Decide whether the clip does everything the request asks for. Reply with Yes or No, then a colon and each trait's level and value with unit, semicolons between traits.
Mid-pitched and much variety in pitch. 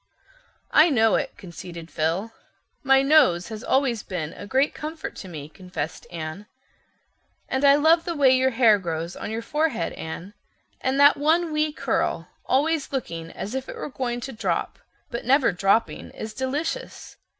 No: high, 245 Hz; wide, 7.8 semitones